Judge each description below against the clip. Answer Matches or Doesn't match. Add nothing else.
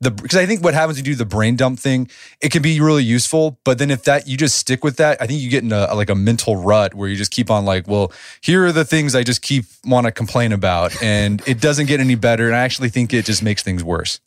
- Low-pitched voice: Matches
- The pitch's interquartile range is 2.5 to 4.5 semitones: Doesn't match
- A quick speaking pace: Matches